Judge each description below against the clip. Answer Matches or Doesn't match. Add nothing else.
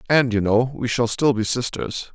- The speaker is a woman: Doesn't match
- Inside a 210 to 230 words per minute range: Matches